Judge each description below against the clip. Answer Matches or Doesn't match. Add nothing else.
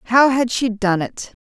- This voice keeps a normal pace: Doesn't match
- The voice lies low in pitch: Doesn't match